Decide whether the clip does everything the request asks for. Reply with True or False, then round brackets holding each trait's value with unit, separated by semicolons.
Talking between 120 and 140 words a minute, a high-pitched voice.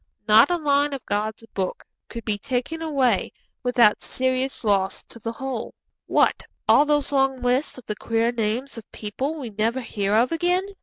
False (175 wpm; 245 Hz)